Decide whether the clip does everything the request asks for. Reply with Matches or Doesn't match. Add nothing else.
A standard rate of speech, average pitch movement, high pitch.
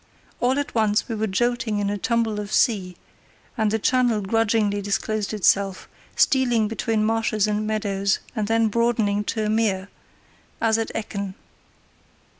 Doesn't match